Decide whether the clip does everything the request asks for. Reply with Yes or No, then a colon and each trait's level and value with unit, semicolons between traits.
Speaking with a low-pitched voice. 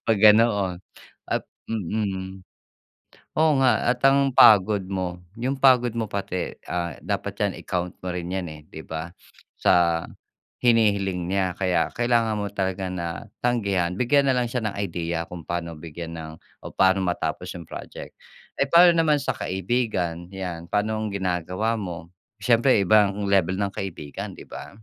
Yes: very low, 95 Hz